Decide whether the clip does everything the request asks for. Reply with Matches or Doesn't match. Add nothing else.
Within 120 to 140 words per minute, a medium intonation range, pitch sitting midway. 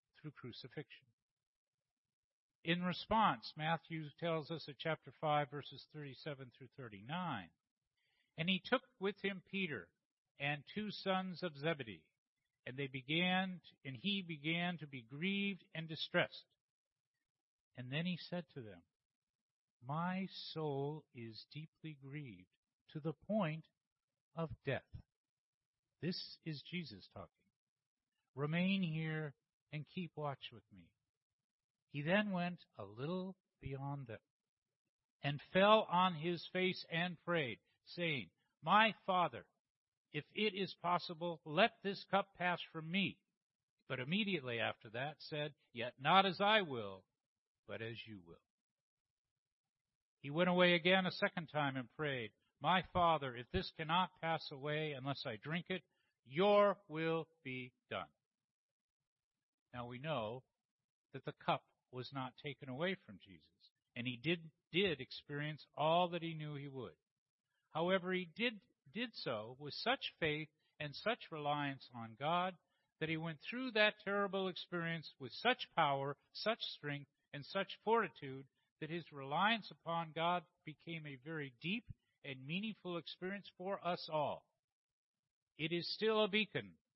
Matches